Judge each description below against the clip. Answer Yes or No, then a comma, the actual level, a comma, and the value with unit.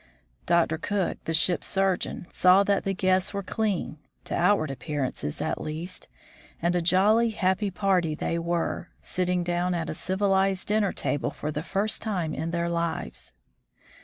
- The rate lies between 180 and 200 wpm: No, average, 160 wpm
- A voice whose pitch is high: No, medium, 180 Hz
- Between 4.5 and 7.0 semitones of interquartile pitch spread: No, average, 2.7 semitones